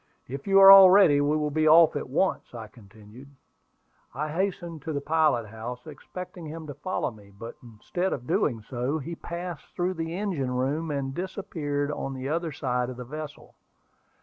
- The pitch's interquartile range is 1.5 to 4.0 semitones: No, average, 5.0 semitones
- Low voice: No, medium, 150 Hz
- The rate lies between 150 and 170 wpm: No, average, 185 wpm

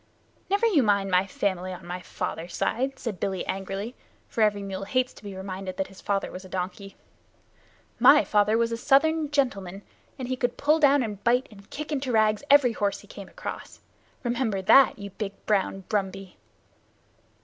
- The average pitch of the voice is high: Yes, high, 205 Hz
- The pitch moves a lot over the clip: No, average, 4.7 semitones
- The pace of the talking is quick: No, average, 180 wpm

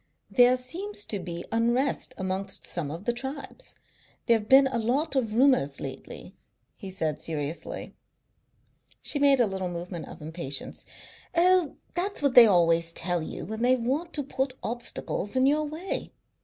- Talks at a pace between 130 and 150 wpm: No, average, 160 wpm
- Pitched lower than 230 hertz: No, high, 235 Hz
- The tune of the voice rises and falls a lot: Yes, wide, 7.6 semitones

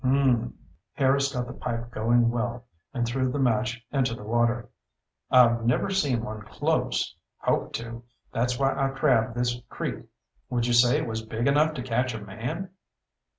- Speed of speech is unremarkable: Yes, average, 170 wpm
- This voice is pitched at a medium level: No, low, 120 Hz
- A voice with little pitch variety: Yes, narrow, 2.0 semitones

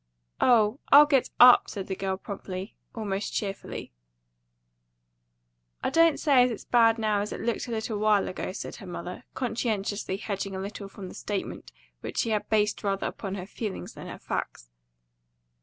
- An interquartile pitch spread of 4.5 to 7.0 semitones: No, average, 2.8 semitones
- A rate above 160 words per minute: Yes, average, 175 wpm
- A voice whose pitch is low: No, high, 210 Hz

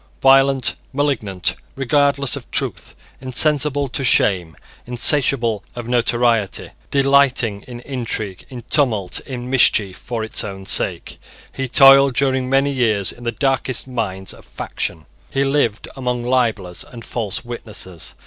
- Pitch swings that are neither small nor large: Yes, average, 3.8 semitones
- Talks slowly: Yes, slow, 130 wpm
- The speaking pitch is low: Yes, low, 125 Hz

